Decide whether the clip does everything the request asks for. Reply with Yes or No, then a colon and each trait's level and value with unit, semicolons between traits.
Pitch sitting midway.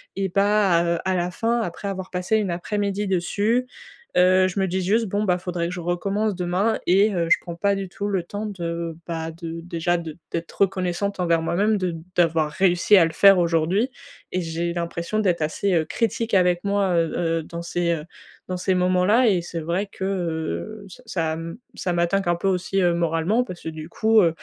Yes: medium, 180 Hz